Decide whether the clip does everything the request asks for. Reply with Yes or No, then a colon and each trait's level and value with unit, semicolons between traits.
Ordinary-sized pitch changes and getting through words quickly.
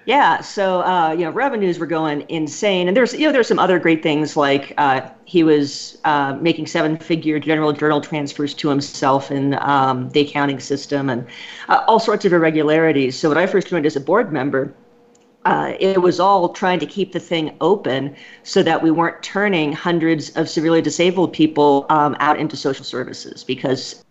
No: average, 3.8 semitones; average, 190 wpm